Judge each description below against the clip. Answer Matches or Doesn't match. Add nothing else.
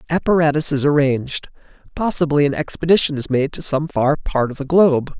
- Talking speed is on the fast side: Doesn't match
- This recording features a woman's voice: Doesn't match